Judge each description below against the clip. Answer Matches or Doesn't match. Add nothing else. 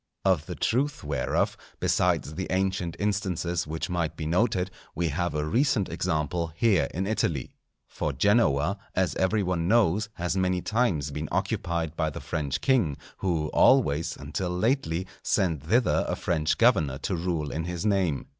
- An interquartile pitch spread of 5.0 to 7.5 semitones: Doesn't match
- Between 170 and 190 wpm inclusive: Doesn't match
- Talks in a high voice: Doesn't match